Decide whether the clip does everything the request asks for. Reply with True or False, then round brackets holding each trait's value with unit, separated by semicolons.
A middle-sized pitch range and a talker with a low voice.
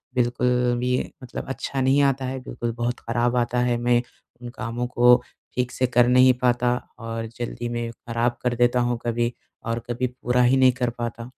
False (0.9 semitones; 120 Hz)